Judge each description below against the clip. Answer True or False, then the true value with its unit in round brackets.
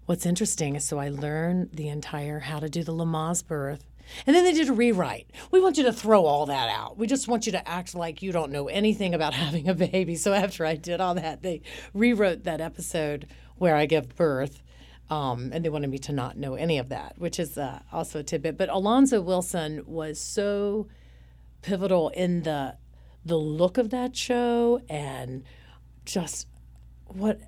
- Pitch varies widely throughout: False (4.8 semitones)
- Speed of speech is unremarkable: True (195 wpm)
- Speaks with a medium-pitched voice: True (165 Hz)